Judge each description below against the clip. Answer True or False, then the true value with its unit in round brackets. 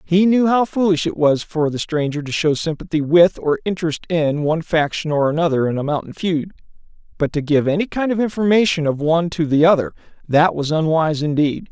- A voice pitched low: False (160 Hz)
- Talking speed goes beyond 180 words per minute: True (200 wpm)